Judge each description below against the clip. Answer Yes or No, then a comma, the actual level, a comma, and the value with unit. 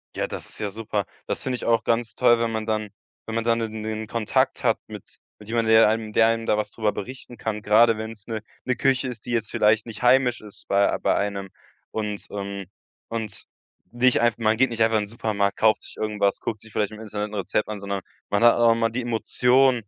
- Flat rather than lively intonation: Yes, narrow, 1.7 semitones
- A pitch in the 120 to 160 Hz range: No, low, 110 Hz